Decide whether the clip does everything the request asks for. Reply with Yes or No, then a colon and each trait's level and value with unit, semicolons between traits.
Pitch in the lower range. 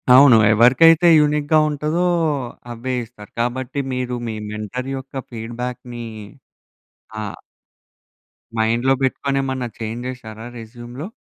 Yes: low, 125 Hz